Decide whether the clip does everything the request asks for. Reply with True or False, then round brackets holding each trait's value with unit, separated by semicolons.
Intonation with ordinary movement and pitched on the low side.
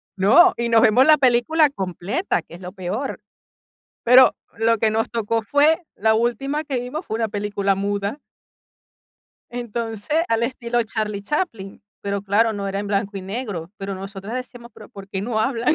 False (3.7 semitones; 225 Hz)